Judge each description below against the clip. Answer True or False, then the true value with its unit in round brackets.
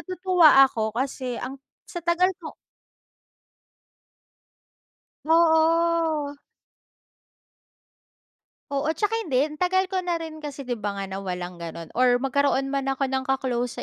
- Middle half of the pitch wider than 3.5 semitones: True (4.9 semitones)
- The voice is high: True (275 Hz)